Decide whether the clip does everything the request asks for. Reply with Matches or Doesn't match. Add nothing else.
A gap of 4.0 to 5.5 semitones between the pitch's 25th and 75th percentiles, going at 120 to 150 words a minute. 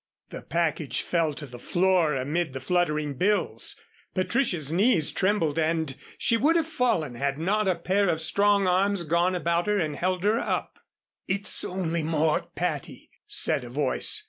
Doesn't match